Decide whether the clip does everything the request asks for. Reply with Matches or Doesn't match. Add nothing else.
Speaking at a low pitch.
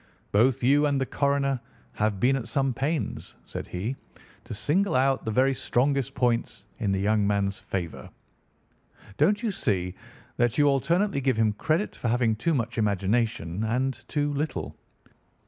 Matches